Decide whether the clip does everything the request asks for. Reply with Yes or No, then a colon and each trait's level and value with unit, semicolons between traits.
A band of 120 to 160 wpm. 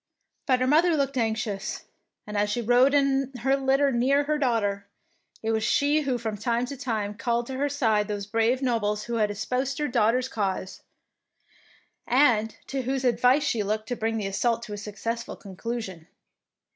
No: average, 185 wpm